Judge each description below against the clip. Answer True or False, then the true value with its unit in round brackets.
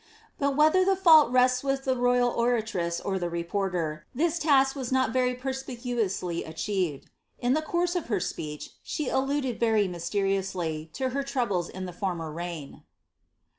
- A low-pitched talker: False (235 Hz)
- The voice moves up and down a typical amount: False (7.0 semitones)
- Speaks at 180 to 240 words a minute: False (165 wpm)